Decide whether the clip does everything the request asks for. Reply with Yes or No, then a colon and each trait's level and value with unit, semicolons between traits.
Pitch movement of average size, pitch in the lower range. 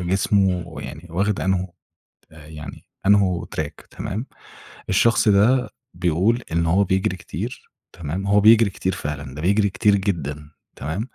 Yes: average, 3.9 semitones; very low, 95 Hz